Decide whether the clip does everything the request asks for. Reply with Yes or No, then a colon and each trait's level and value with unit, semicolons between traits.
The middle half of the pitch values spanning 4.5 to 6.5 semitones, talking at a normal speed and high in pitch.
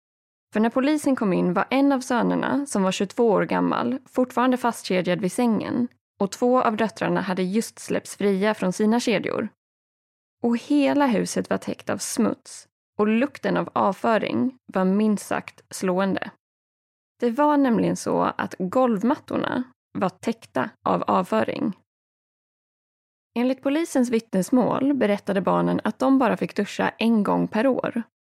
Yes: average, 4.8 semitones; average, 145 wpm; high, 235 Hz